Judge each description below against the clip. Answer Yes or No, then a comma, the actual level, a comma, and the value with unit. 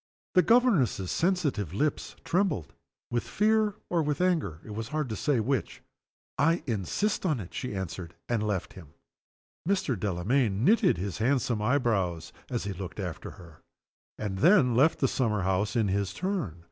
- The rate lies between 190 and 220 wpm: No, average, 160 wpm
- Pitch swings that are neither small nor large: No, wide, 8.4 semitones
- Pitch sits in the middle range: No, low, 115 Hz